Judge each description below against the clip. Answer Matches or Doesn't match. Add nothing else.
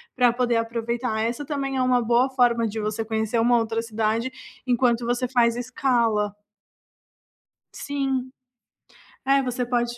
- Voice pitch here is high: Matches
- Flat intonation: Matches